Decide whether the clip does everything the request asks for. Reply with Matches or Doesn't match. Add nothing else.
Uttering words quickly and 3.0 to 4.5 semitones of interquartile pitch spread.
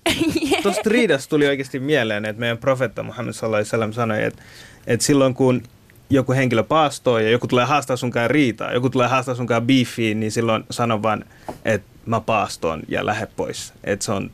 Matches